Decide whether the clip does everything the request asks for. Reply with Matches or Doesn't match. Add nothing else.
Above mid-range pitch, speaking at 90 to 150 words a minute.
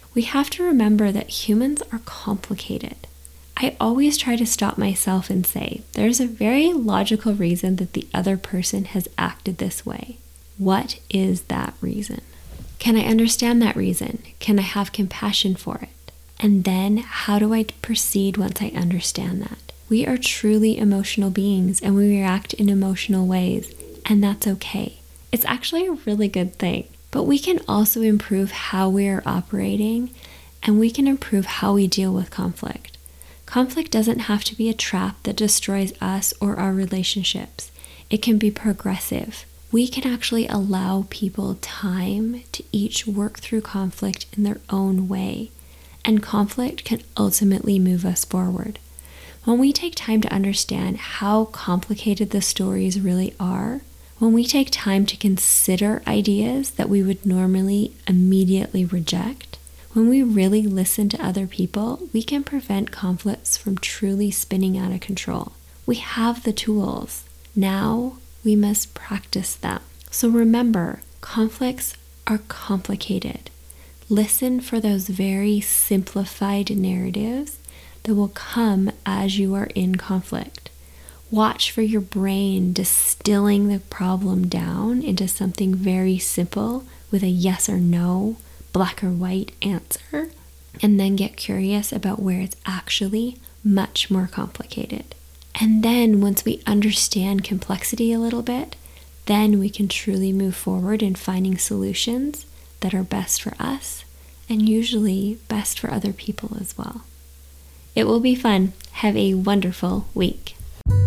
Matches